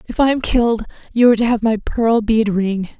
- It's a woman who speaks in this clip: Yes, female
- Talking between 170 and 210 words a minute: No, fast, 240 wpm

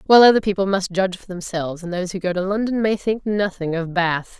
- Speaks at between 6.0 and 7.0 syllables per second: Yes, 6.2 syllables/s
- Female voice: Yes, female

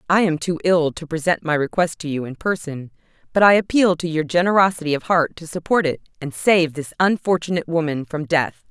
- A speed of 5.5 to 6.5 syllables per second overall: Yes, 5.6 syllables/s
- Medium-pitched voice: Yes, medium, 165 Hz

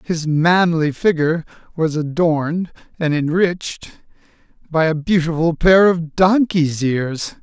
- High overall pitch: No, medium, 165 Hz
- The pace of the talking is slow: Yes, slow, 115 wpm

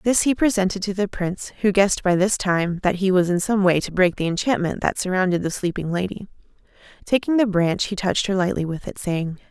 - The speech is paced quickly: Yes, fast, 225 wpm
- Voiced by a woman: Yes, female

